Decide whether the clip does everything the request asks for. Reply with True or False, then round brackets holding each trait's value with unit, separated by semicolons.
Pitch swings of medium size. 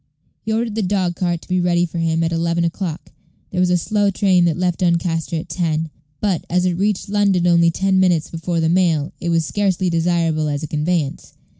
False (2.0 semitones)